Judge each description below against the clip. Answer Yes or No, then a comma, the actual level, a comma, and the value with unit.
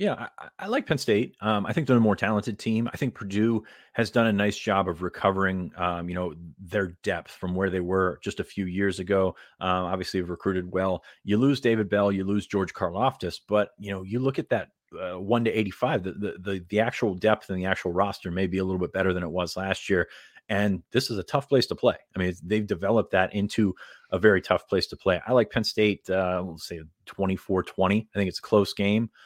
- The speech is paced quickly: Yes, fast, 240 wpm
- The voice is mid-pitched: No, low, 100 Hz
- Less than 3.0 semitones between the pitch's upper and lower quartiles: Yes, narrow, 2.5 semitones